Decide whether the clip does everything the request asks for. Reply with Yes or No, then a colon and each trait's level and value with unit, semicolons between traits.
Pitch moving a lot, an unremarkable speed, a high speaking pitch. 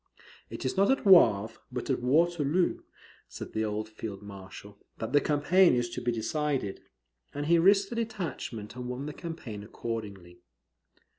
No: wide, 7.5 semitones; average, 160 wpm; low, 125 Hz